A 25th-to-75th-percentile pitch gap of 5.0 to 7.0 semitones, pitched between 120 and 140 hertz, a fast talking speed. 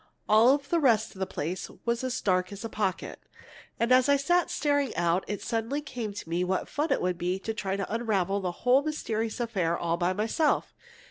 No: wide, 5.5 semitones; high, 220 Hz; fast, 210 wpm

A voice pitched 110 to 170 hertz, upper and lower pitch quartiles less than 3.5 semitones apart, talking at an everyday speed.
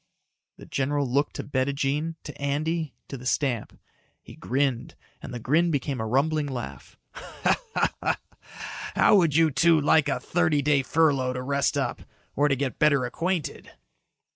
Yes: medium, 140 Hz; average, 2.7 semitones; average, 150 wpm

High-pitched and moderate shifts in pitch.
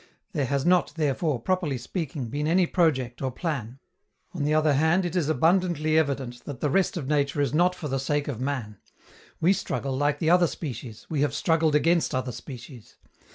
No: medium, 150 Hz; average, 3.8 semitones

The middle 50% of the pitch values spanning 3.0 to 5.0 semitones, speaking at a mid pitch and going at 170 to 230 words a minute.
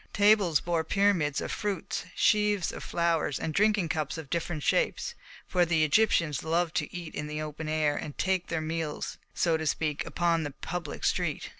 No: narrow, 2.6 semitones; medium, 165 Hz; average, 180 wpm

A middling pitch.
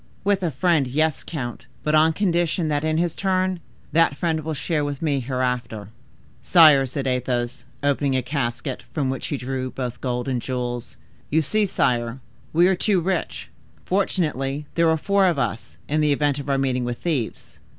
Yes: medium, 145 Hz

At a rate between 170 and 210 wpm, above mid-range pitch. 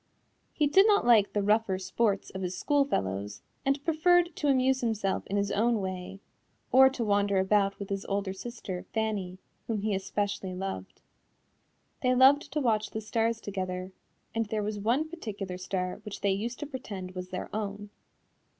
Yes: average, 175 wpm; high, 205 Hz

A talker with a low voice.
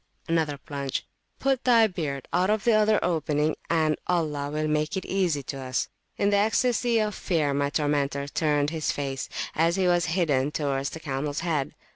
No: medium, 155 Hz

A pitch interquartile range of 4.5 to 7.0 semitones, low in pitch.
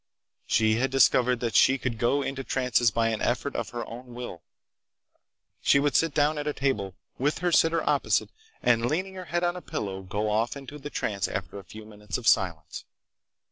Yes: average, 4.8 semitones; low, 125 Hz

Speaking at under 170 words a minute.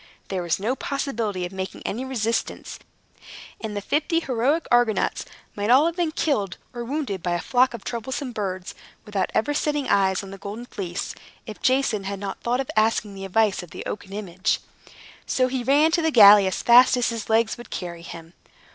No: average, 195 wpm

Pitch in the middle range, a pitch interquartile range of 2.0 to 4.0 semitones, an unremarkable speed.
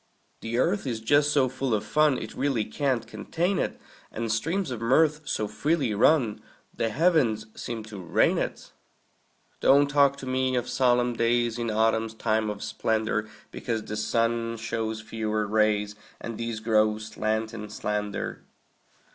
No: low, 115 Hz; average, 3.4 semitones; average, 155 wpm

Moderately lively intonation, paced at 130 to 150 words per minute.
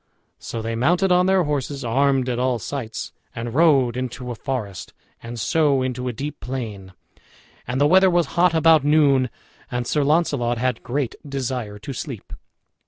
No: average, 3.7 semitones; average, 170 wpm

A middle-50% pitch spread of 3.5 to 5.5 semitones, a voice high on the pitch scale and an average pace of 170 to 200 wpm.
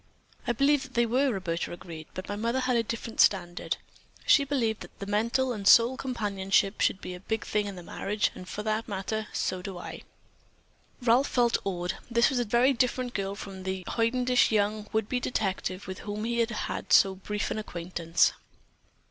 Yes: average, 3.8 semitones; high, 215 Hz; average, 185 wpm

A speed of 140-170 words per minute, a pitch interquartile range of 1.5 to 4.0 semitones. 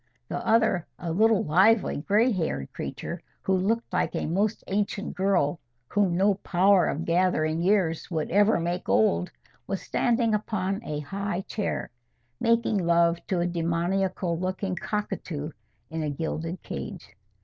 Yes: average, 145 wpm; average, 3.4 semitones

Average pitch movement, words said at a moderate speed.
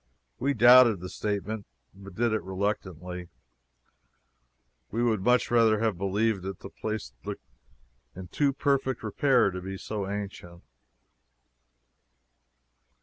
No: average, 3.6 semitones; slow, 120 wpm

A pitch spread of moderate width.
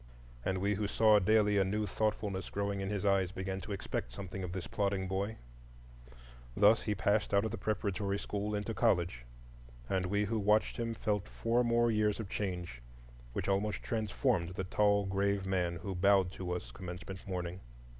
No: narrow, 2.0 semitones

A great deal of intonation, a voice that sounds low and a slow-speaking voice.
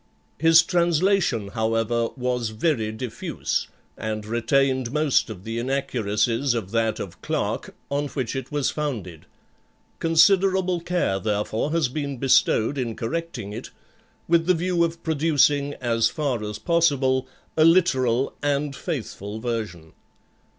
Yes: wide, 6.0 semitones; low, 130 Hz; slow, 130 wpm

